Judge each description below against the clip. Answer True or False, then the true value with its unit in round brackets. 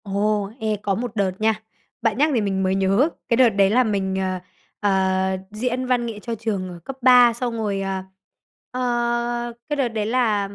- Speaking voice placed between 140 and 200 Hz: False (215 Hz)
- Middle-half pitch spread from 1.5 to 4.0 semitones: True (3.6 semitones)